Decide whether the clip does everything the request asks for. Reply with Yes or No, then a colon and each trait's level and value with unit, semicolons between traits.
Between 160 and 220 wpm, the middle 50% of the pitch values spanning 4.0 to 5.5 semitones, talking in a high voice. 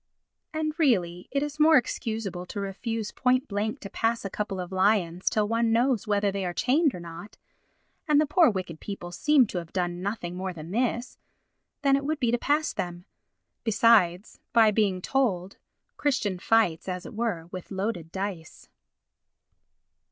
Yes: average, 165 wpm; average, 5.2 semitones; high, 210 Hz